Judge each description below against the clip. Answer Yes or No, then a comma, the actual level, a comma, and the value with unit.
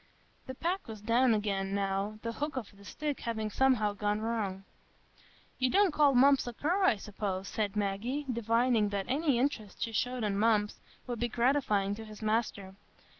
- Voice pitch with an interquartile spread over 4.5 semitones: No, average, 3.9 semitones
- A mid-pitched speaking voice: No, high, 225 Hz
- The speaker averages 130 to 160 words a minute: No, average, 175 wpm